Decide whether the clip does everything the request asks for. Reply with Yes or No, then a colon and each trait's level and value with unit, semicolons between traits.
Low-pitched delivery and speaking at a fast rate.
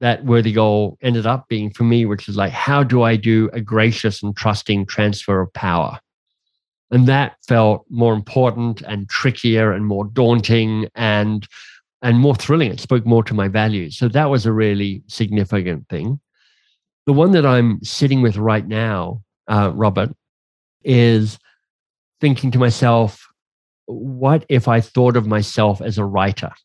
No: low, 110 Hz; average, 160 wpm